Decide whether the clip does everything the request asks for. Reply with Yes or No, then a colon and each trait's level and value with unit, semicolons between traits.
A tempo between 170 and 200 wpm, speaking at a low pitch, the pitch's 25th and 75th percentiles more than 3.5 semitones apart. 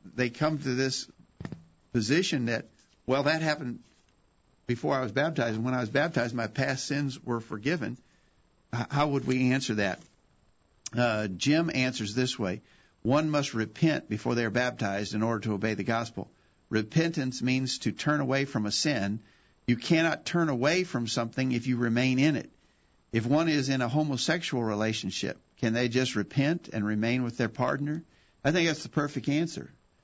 Yes: average, 175 wpm; low, 125 Hz; average, 4.3 semitones